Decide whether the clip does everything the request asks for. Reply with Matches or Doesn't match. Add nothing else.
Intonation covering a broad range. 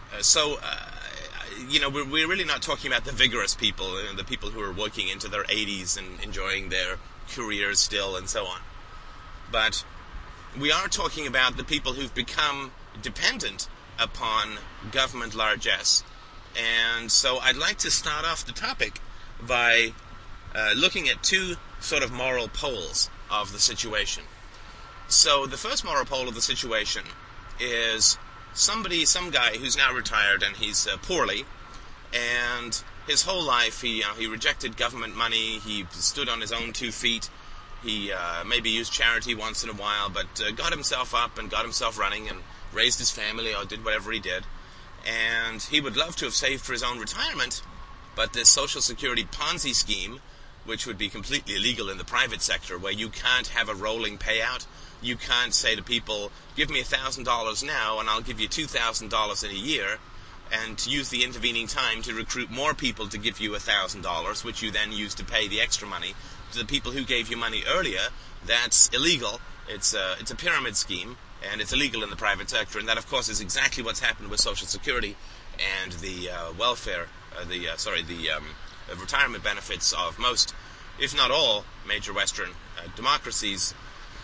Doesn't match